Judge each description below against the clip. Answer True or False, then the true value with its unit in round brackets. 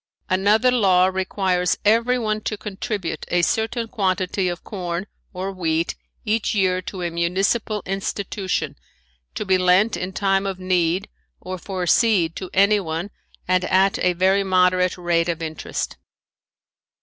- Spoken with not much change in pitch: True (2.1 semitones)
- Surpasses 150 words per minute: False (135 wpm)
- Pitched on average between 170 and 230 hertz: True (185 Hz)